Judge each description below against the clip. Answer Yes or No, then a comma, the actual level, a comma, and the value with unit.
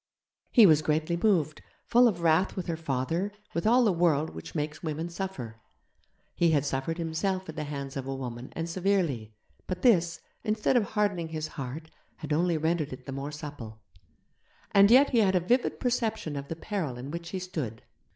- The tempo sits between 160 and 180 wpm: No, average, 190 wpm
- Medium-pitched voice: Yes, medium, 165 Hz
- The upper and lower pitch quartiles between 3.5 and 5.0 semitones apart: Yes, average, 4.6 semitones